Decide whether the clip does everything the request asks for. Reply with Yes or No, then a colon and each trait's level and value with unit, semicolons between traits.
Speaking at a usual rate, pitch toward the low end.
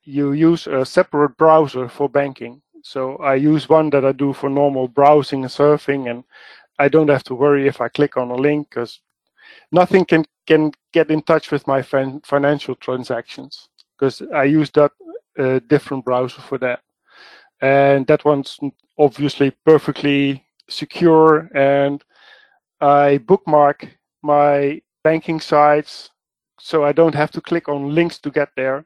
No: average, 160 wpm; medium, 145 Hz